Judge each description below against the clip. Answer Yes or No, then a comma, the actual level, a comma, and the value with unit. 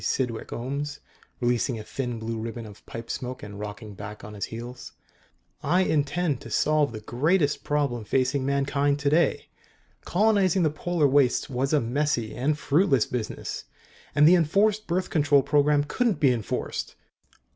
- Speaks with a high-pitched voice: No, medium, 140 Hz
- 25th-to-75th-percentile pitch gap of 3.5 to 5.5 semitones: Yes, average, 4.3 semitones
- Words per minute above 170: No, average, 155 wpm